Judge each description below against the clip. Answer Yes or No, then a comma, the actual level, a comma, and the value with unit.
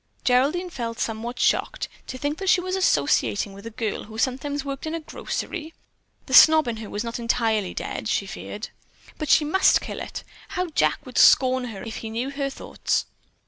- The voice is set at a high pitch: Yes, very high, 255 Hz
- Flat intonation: No, wide, 5.5 semitones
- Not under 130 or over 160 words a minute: No, average, 195 wpm